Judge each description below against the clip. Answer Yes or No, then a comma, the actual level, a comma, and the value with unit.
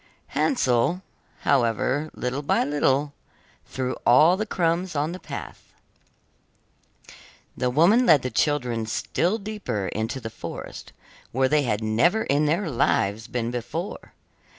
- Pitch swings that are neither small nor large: No, wide, 5.9 semitones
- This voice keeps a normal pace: No, slow, 130 wpm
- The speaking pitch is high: No, medium, 140 Hz